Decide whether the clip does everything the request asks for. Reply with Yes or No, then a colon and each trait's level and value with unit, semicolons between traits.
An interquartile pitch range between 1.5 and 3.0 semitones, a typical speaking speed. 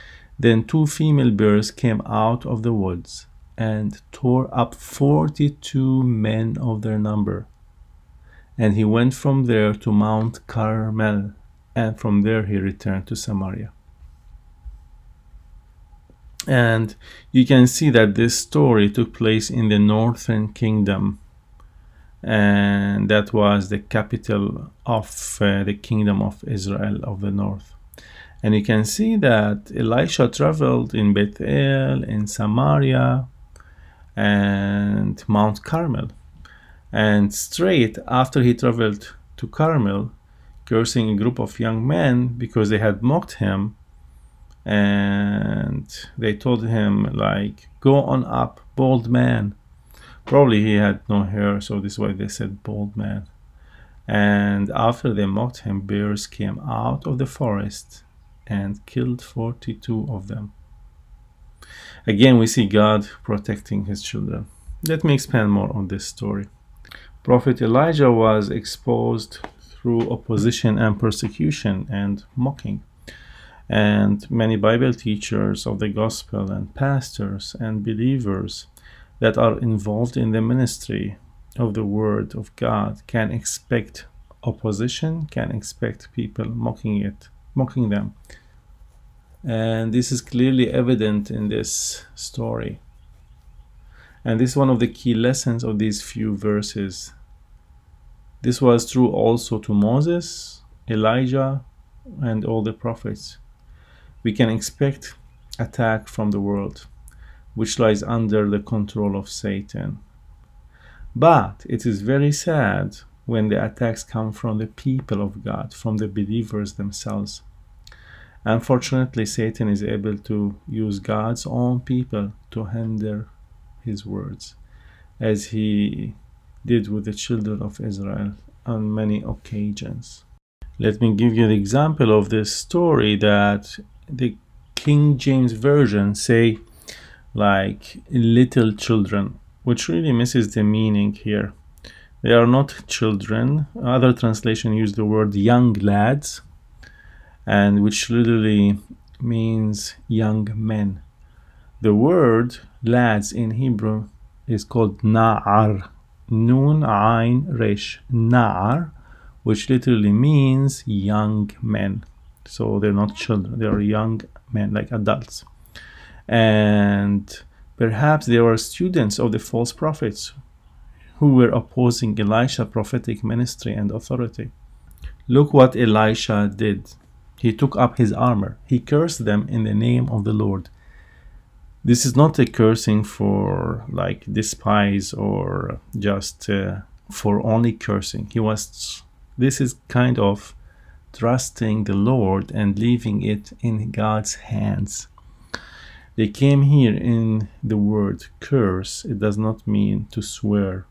No: average, 2.7 semitones; slow, 125 wpm